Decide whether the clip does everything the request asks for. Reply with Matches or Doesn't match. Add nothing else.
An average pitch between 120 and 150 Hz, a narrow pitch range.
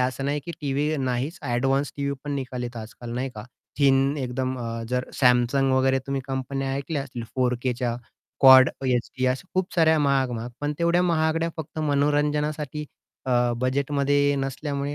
Matches